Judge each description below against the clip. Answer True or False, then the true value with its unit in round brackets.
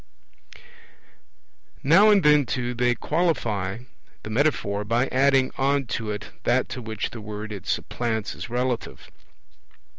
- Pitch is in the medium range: False (120 Hz)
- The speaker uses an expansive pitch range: False (4.2 semitones)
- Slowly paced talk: True (130 wpm)